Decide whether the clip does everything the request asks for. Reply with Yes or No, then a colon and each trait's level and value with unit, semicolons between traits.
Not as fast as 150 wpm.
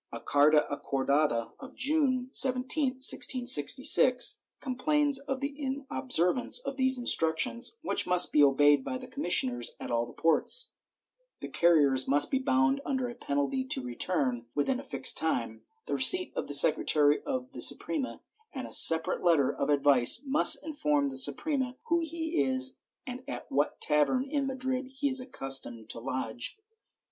No: average, 155 wpm